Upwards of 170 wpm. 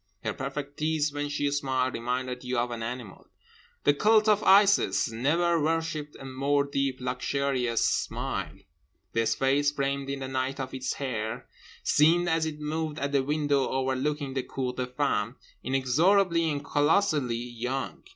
No: average, 155 wpm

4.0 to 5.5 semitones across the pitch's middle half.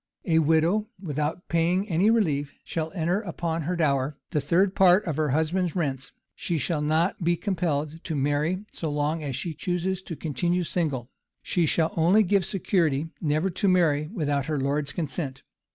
No: average, 3.3 semitones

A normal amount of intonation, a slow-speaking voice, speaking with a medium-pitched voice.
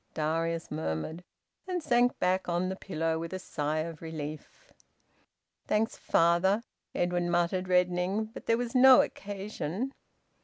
Yes: average, 4.3 semitones; slow, 130 wpm; medium, 180 Hz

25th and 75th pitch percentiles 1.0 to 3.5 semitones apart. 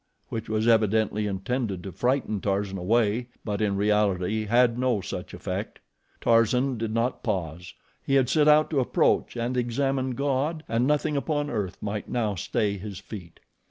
No: average, 3.9 semitones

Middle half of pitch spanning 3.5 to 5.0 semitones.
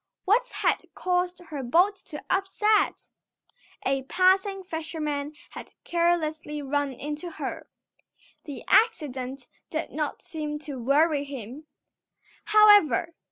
Yes: average, 4.2 semitones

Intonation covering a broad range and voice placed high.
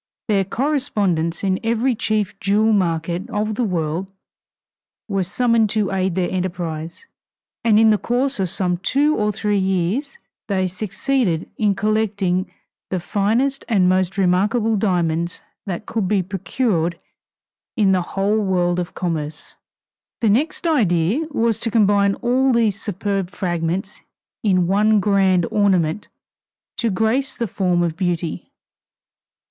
No: average, 3.6 semitones; high, 195 Hz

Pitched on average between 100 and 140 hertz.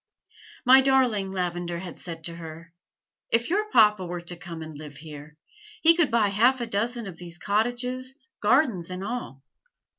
No: high, 195 Hz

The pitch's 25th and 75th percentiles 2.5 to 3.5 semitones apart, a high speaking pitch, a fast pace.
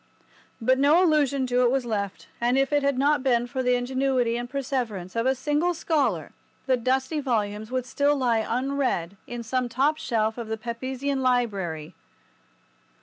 No: average, 2.9 semitones; very high, 255 Hz; average, 170 wpm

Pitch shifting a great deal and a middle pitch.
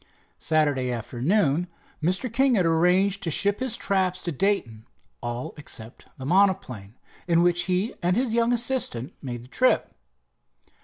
Yes: wide, 7.4 semitones; medium, 175 Hz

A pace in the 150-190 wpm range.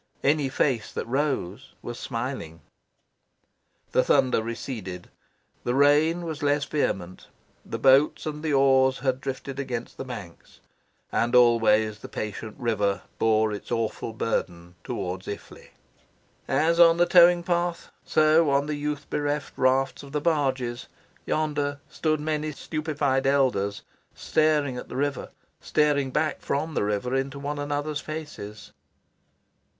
No: slow, 135 wpm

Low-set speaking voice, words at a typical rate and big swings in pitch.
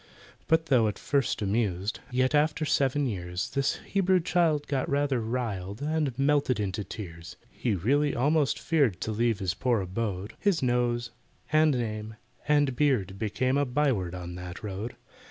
Yes: low, 125 Hz; average, 155 wpm; wide, 6.1 semitones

